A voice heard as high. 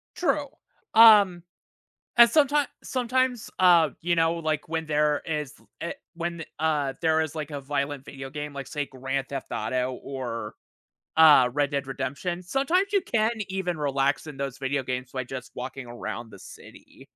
No: medium, 150 Hz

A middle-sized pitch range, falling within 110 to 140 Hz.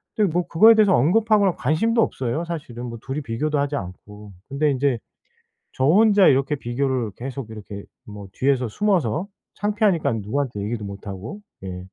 No: wide, 7.6 semitones; low, 135 Hz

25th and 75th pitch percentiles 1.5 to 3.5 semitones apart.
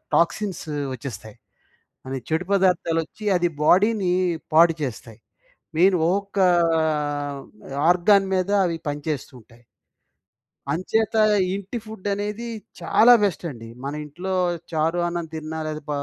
No: average, 4.9 semitones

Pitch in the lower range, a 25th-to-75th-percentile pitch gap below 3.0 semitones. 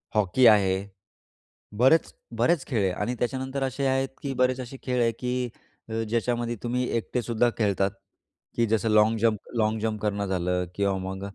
No: low, 115 Hz; average, 3.4 semitones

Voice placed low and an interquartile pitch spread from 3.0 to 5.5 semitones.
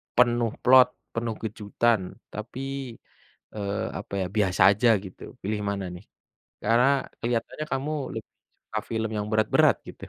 No: low, 110 Hz; narrow, 2.5 semitones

